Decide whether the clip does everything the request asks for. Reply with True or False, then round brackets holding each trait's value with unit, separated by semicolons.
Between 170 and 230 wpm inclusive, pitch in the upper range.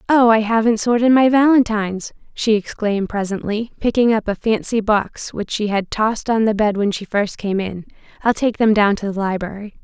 True (200 wpm; 215 Hz)